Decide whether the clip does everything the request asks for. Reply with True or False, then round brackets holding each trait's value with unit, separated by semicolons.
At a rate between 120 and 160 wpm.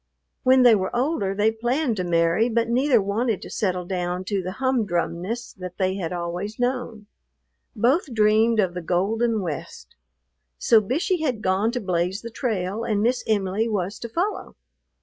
False (170 wpm)